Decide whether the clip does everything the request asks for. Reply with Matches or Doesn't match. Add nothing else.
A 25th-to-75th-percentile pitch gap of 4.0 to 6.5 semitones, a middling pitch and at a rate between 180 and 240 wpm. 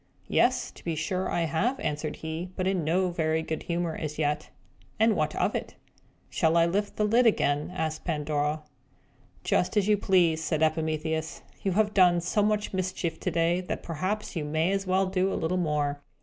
Doesn't match